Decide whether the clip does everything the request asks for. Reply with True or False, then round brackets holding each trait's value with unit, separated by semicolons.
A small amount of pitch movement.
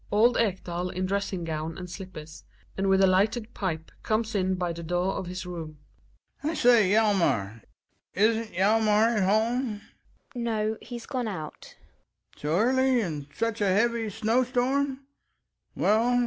False (4.3 semitones)